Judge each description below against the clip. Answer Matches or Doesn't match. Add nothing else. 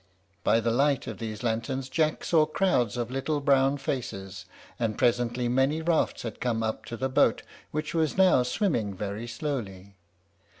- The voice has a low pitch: Matches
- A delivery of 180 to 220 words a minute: Doesn't match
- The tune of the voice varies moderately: Matches